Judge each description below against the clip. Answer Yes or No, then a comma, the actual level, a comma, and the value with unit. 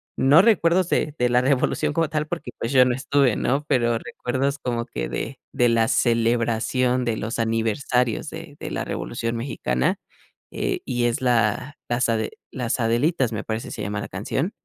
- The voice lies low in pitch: Yes, low, 120 Hz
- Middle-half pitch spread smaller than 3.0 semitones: No, average, 3.4 semitones